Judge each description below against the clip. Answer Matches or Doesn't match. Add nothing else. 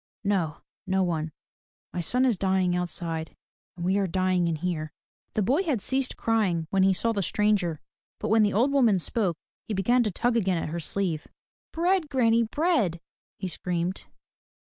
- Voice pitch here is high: Matches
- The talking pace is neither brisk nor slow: Matches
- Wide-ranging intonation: Doesn't match